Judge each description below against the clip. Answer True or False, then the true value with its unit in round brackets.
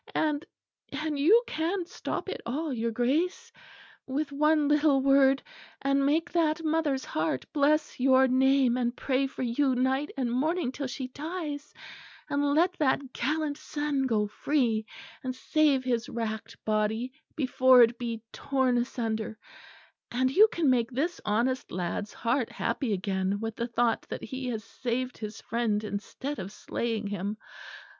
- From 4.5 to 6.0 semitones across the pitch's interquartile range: False (4.0 semitones)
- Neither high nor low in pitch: False (260 Hz)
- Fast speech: False (150 wpm)